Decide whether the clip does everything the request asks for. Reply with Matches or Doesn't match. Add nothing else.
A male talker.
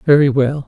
Matches